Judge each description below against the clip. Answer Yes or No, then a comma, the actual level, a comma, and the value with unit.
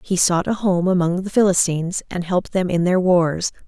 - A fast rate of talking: Yes, fast, 210 wpm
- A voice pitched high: No, medium, 180 Hz